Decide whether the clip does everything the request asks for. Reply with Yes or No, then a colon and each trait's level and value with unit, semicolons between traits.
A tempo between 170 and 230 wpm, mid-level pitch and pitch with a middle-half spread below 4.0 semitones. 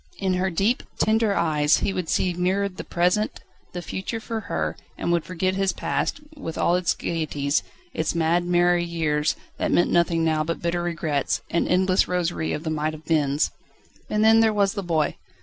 Yes: average, 190 wpm; medium, 175 Hz; average, 2.9 semitones